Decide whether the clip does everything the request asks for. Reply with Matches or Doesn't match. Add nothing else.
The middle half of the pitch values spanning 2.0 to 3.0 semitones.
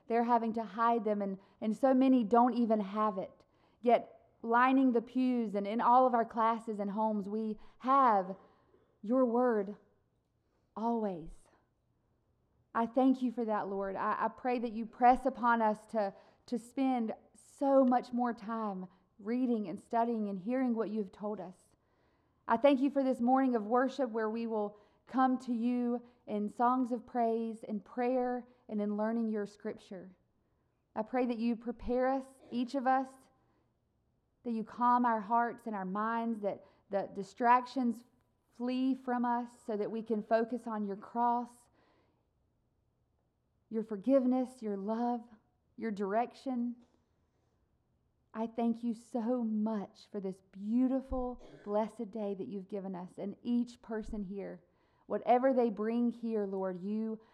Matches